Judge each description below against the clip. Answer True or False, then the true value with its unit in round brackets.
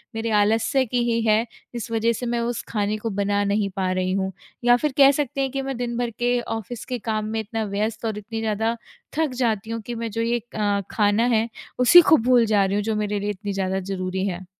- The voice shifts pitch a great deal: False (2.8 semitones)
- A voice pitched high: True (220 Hz)